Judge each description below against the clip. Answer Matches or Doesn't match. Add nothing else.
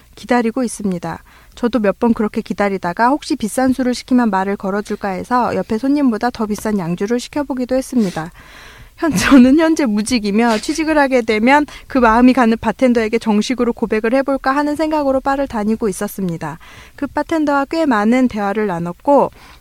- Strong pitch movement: Doesn't match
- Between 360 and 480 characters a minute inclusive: Matches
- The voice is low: Doesn't match